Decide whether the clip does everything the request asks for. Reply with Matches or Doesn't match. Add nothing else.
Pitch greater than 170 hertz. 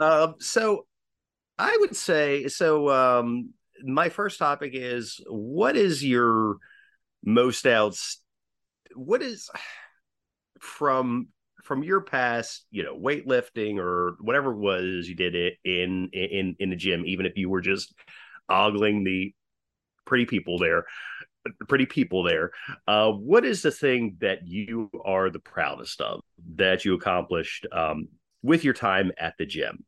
Doesn't match